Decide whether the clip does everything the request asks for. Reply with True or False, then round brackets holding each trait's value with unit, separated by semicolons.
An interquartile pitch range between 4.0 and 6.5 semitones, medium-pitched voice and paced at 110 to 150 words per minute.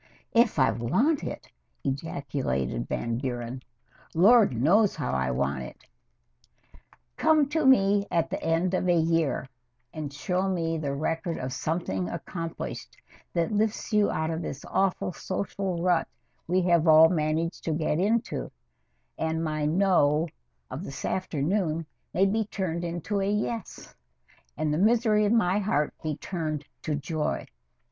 True (4.6 semitones; 165 Hz; 145 wpm)